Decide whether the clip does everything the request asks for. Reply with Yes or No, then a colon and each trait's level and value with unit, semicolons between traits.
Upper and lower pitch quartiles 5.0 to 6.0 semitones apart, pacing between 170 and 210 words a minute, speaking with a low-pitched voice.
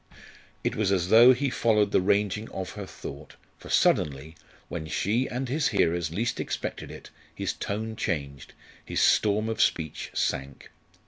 No: wide, 5.6 semitones; average, 155 wpm; low, 100 Hz